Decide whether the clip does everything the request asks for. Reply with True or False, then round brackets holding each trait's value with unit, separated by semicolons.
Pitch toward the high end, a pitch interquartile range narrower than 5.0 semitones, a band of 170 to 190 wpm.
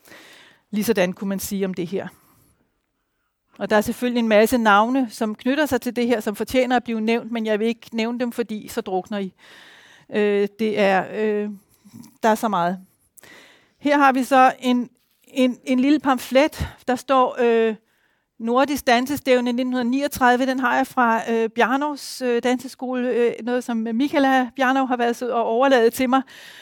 True (240 Hz; 2.7 semitones; 175 wpm)